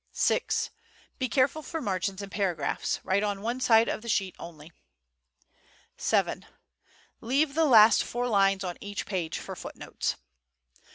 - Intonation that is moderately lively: Yes, average, 4.3 semitones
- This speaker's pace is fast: No, average, 145 wpm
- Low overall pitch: No, high, 205 Hz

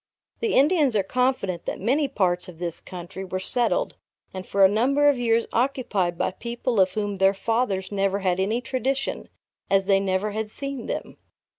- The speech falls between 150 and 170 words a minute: No, average, 180 wpm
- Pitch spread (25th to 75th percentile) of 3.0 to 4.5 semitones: No, average, 5.0 semitones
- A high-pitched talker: Yes, high, 205 Hz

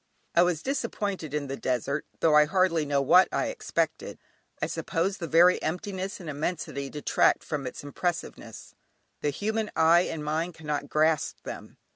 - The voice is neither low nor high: Yes, medium, 160 Hz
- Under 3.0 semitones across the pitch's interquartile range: No, average, 3.6 semitones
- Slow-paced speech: No, average, 160 wpm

